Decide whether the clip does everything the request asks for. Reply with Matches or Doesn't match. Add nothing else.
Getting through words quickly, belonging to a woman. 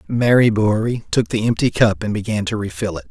Doesn't match